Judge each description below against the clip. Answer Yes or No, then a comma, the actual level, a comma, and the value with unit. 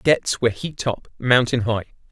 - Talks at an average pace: Yes, average, 170 wpm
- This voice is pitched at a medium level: No, low, 115 Hz